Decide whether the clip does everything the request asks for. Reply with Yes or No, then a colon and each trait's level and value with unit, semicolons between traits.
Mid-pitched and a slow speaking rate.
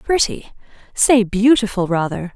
No: high, 215 Hz; slow, 100 wpm